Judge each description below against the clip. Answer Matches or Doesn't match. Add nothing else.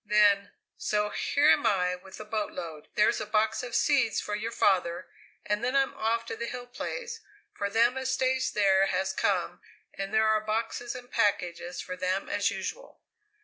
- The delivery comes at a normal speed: Matches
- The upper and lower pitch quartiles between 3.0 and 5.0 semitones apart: Matches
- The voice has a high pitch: Matches